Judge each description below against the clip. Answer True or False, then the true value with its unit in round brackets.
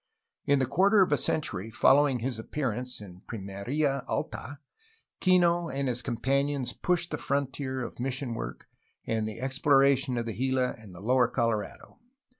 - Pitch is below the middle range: True (130 Hz)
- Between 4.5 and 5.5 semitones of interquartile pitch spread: False (3.5 semitones)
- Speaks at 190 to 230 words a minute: False (150 wpm)